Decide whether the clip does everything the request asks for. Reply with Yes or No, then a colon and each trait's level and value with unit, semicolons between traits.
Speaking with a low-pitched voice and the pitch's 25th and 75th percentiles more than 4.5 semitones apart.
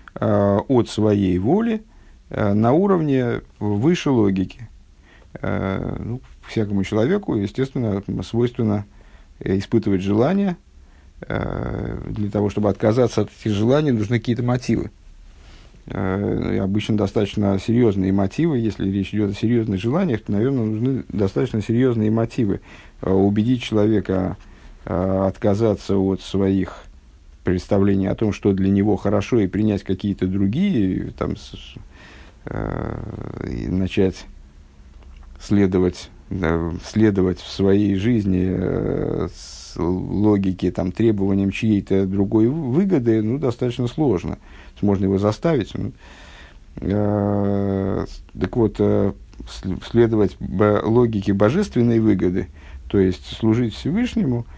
No: low, 100 Hz; average, 3.4 semitones